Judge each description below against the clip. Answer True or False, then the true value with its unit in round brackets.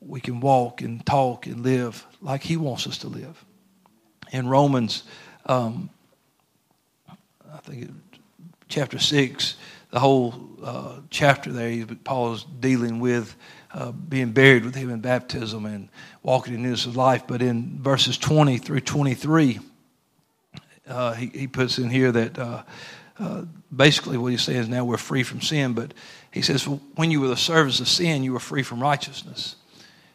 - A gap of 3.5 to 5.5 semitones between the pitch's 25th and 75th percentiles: False (2.6 semitones)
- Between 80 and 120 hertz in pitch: False (130 Hz)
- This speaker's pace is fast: False (165 wpm)